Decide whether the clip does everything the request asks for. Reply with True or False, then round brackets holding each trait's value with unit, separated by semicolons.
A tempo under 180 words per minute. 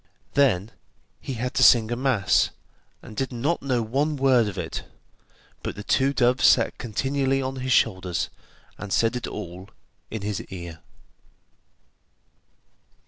True (140 wpm)